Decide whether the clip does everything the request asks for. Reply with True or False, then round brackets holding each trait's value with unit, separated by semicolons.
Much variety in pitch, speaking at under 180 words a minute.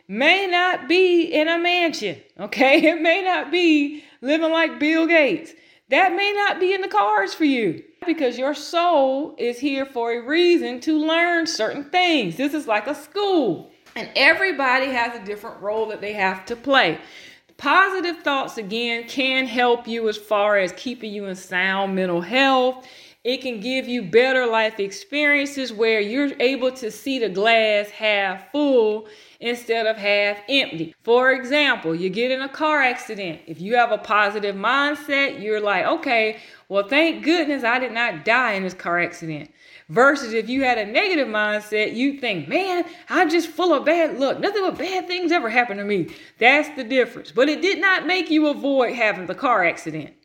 False (6.6 semitones; 185 wpm)